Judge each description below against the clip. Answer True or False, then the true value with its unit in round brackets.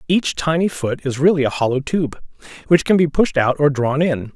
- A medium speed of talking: False (220 wpm)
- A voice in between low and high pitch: True (150 Hz)